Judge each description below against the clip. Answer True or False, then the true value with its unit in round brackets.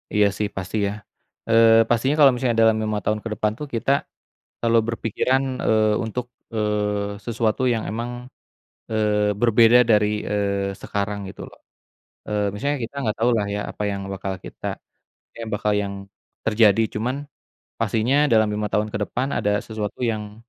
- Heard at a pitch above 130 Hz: False (110 Hz)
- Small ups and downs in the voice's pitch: True (1.8 semitones)